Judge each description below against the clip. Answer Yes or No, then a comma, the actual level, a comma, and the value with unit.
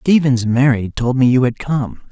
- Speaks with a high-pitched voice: No, low, 130 Hz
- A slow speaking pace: No, average, 200 wpm